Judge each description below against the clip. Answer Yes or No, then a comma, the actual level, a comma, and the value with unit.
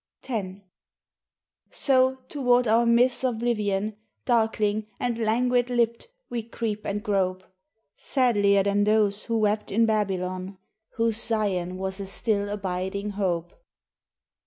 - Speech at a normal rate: No, slow, 115 wpm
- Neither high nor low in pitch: No, high, 215 Hz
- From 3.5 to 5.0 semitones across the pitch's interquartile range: No, average, 2.9 semitones